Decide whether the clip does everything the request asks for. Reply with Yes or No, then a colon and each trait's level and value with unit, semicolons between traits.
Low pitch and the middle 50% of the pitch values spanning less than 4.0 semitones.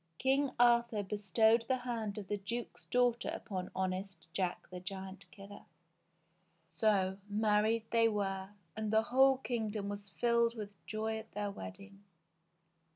No: high, 210 Hz; average, 3.0 semitones